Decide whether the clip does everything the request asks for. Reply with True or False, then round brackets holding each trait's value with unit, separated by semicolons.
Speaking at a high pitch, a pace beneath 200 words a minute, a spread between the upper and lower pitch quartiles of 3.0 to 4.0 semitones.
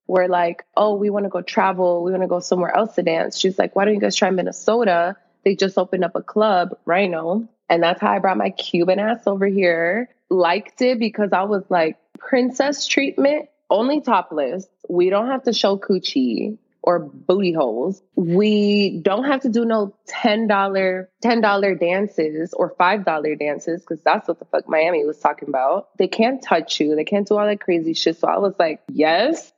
False (195 Hz; 205 wpm; 3.7 semitones)